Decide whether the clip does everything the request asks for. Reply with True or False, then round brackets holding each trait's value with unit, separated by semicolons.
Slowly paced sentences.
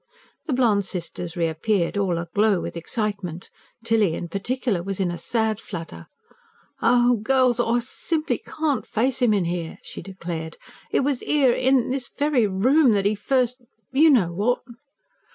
False (155 wpm)